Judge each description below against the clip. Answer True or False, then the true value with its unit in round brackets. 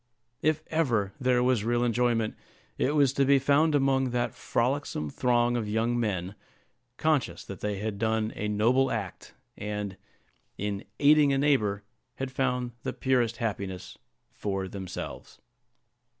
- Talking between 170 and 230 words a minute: False (140 wpm)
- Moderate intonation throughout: True (4.3 semitones)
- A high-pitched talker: False (120 Hz)